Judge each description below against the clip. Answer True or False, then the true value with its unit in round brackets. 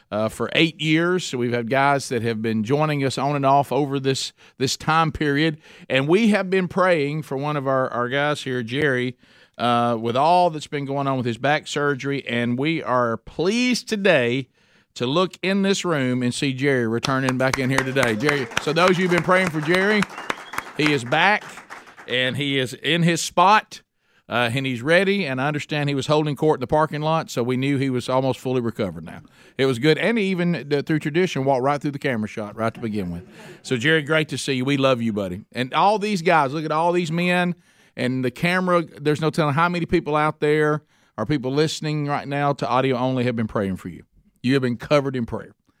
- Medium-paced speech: False (225 wpm)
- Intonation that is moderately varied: True (4.0 semitones)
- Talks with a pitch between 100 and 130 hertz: False (140 Hz)